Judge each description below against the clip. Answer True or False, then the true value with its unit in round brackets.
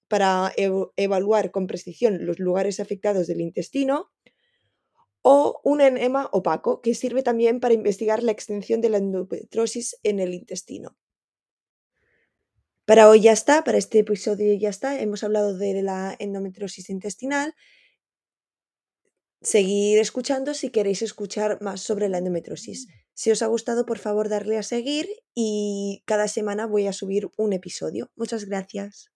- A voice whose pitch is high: True (210 Hz)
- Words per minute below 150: True (140 wpm)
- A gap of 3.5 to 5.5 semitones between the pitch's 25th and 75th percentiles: False (2.9 semitones)